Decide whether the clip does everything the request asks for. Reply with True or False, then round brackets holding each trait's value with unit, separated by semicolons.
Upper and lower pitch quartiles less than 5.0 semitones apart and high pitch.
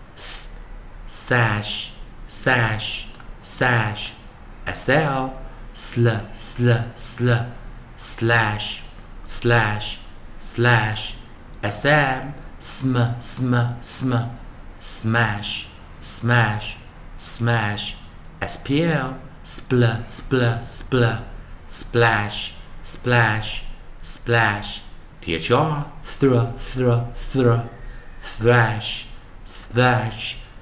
False (2.8 semitones; 115 Hz)